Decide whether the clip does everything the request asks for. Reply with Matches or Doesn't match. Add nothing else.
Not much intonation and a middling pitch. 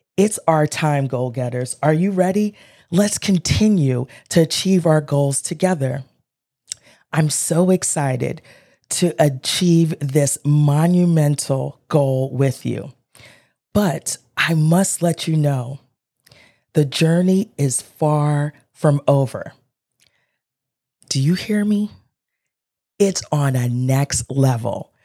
Doesn't match